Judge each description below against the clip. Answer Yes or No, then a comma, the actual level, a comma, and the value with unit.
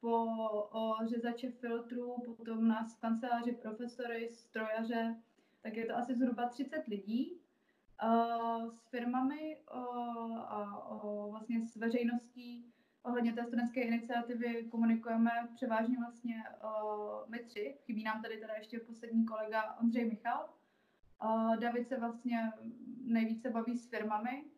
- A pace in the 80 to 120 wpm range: Yes, slow, 115 wpm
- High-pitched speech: Yes, high, 235 Hz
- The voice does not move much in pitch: Yes, narrow, 1.2 semitones